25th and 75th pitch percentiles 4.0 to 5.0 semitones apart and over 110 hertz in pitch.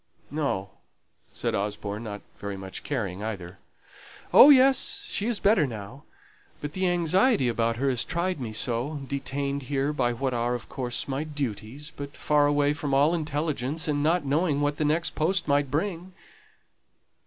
Yes: average, 4.6 semitones; medium, 140 Hz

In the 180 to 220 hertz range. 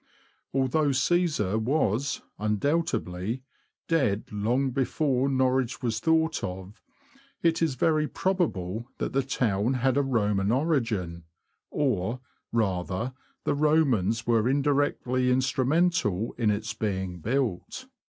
No: low, 125 Hz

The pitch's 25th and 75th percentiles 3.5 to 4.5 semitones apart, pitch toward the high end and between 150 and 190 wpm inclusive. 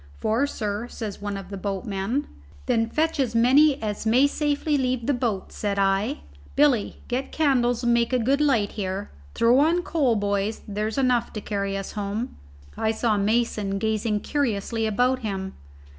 Yes: average, 4.2 semitones; high, 225 Hz; average, 170 wpm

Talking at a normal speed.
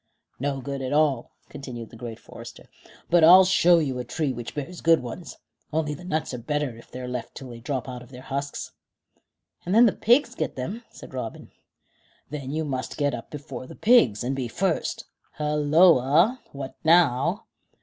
Yes: average, 185 wpm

